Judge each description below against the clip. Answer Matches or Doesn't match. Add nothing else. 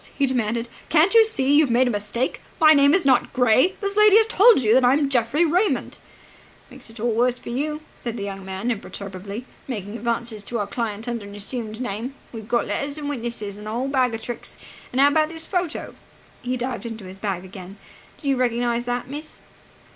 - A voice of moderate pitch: Doesn't match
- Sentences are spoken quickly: Matches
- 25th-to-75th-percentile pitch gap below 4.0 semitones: Doesn't match